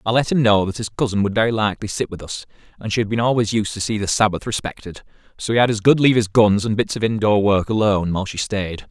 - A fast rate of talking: Yes, fast, 275 wpm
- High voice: No, low, 105 Hz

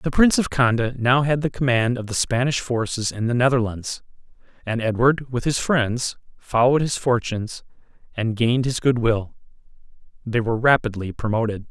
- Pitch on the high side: No, low, 120 Hz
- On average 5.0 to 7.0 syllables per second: Yes, 5.3 syllables/s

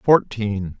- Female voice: No, male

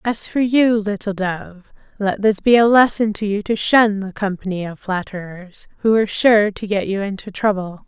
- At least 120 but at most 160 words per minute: No, average, 200 wpm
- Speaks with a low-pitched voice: No, high, 205 Hz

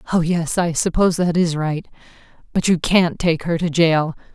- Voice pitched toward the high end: No, medium, 165 Hz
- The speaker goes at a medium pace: Yes, average, 195 wpm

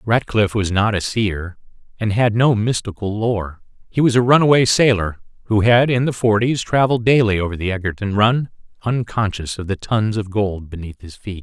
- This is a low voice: Yes, low, 110 Hz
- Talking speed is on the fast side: No, average, 185 wpm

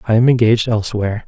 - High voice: No, low, 115 Hz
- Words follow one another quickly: No, average, 190 wpm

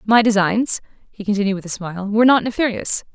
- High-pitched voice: Yes, high, 210 Hz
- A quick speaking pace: No, average, 190 wpm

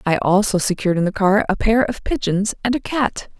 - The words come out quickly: Yes, fast, 230 wpm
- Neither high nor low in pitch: No, high, 205 Hz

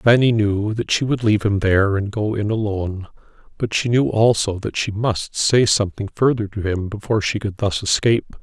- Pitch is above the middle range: No, low, 105 Hz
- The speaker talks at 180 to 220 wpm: Yes, fast, 205 wpm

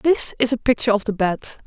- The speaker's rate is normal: No, fast, 250 wpm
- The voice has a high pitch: Yes, high, 230 Hz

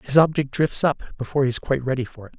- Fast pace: Yes, fast, 275 wpm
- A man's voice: Yes, male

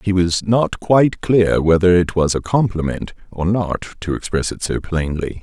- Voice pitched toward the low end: Yes, very low, 95 Hz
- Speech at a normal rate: Yes, average, 190 wpm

